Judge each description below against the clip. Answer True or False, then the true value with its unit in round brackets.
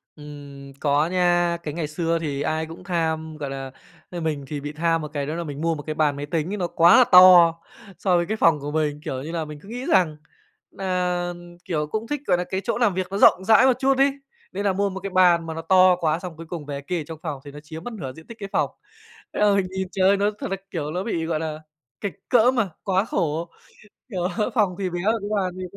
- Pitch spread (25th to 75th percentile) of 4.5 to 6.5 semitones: False (3.8 semitones)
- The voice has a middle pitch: True (170 Hz)